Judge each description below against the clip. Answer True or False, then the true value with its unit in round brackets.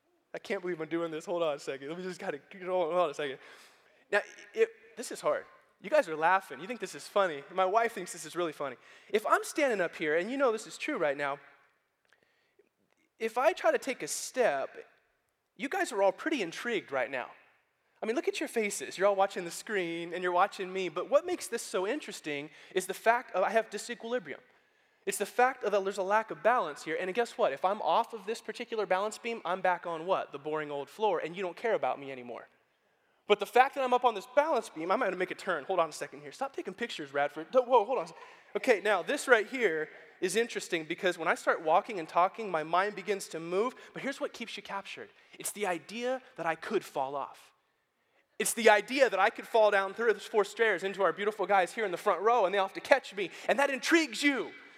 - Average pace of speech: False (250 wpm)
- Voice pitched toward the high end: True (205 Hz)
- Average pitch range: False (5.8 semitones)